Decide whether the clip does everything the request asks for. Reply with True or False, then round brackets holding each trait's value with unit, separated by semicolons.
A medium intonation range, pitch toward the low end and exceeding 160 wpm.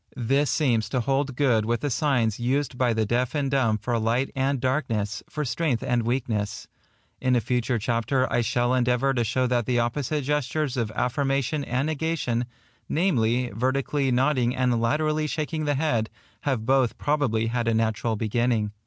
True (3.0 semitones; 125 Hz; 175 wpm)